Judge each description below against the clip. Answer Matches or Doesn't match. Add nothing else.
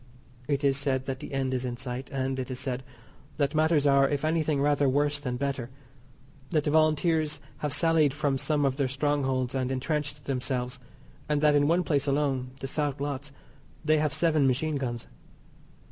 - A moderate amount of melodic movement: Doesn't match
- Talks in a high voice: Doesn't match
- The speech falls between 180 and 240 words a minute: Matches